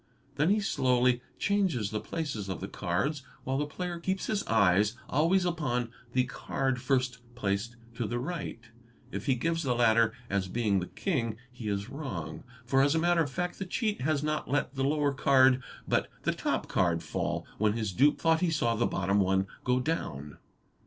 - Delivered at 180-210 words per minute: Yes, average, 190 wpm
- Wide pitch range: Yes, wide, 6.2 semitones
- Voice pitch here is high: No, low, 130 Hz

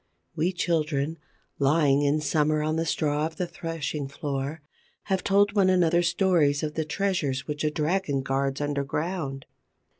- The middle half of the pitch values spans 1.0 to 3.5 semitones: Yes, average, 3.2 semitones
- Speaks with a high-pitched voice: No, medium, 155 Hz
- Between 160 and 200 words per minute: No, average, 150 wpm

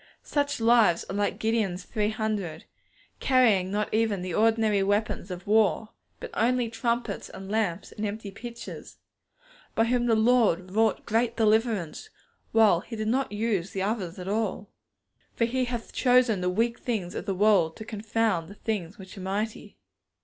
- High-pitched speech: Yes, high, 215 Hz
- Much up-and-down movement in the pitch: No, average, 2.9 semitones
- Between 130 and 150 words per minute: No, average, 165 wpm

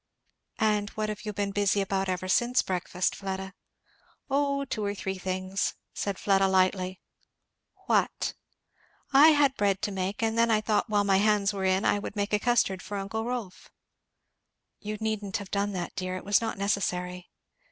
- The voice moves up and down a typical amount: No, narrow, 2.1 semitones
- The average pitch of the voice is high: Yes, high, 200 Hz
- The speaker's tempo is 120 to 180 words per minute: Yes, average, 175 wpm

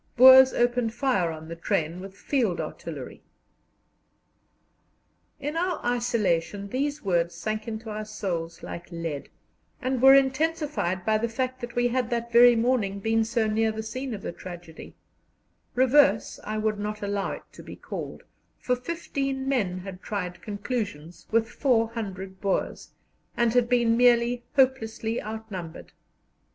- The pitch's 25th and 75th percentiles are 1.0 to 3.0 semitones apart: No, average, 4.3 semitones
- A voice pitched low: No, high, 225 Hz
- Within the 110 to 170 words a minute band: Yes, average, 145 wpm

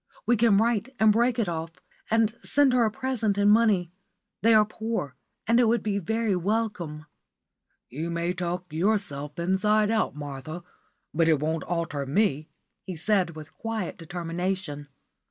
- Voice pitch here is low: No, high, 190 Hz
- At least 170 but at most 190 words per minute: No, average, 155 wpm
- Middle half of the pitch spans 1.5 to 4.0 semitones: No, average, 5.1 semitones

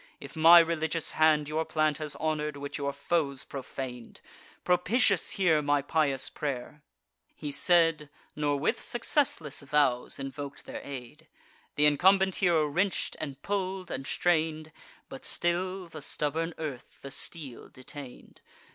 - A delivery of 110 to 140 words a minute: Yes, slow, 135 wpm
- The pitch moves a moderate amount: Yes, average, 3.2 semitones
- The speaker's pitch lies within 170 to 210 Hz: No, medium, 155 Hz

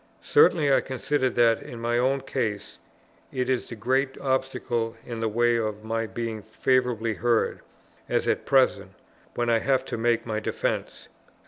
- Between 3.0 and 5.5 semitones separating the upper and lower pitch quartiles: No, narrow, 2.6 semitones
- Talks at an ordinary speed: Yes, average, 160 wpm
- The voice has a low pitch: Yes, low, 120 Hz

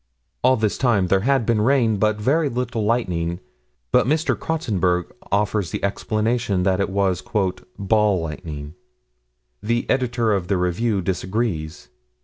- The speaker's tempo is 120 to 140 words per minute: Yes, slow, 135 wpm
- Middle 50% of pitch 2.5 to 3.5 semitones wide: No, average, 4.4 semitones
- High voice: No, low, 105 Hz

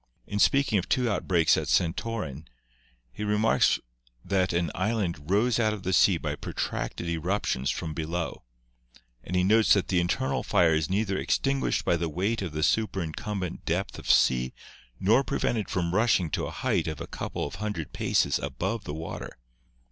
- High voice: No, very low, 90 Hz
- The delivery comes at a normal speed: Yes, average, 175 wpm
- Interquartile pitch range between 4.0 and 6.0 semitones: Yes, average, 4.6 semitones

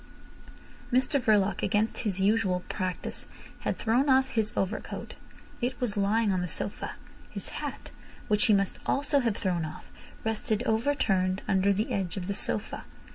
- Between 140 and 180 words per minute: Yes, average, 155 wpm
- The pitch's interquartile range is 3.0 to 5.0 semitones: Yes, average, 3.3 semitones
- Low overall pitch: No, high, 210 Hz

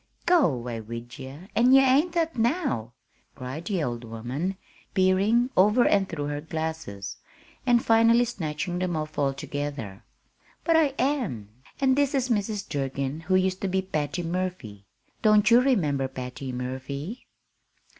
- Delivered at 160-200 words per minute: No, average, 145 wpm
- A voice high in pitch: No, medium, 175 Hz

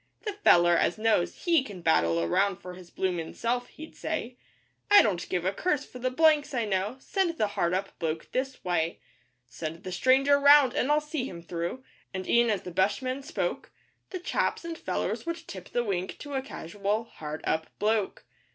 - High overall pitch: Yes, high, 215 Hz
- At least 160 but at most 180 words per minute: No, average, 195 wpm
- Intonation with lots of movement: Yes, wide, 8.0 semitones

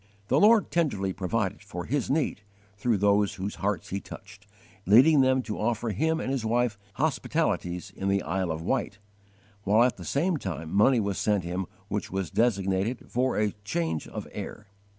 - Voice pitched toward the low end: Yes, low, 105 Hz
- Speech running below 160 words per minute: No, average, 175 wpm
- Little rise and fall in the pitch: No, average, 4.8 semitones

